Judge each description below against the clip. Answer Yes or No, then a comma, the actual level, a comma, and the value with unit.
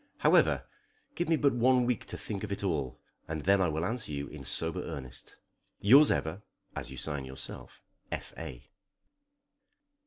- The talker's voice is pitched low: Yes, very low, 90 Hz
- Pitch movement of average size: No, wide, 8.9 semitones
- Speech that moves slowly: No, average, 165 wpm